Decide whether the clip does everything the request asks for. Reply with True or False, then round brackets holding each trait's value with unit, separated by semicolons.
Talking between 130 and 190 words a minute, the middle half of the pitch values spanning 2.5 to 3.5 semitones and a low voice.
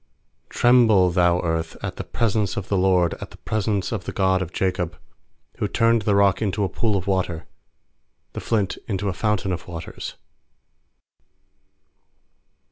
True (160 wpm; 2.8 semitones; 95 Hz)